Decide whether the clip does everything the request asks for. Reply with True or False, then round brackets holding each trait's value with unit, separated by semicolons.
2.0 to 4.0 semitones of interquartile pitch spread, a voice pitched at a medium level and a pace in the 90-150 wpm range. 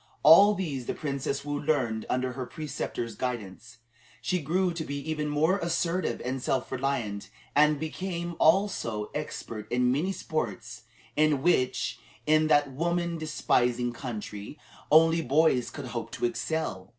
False (4.5 semitones; 145 Hz; 140 wpm)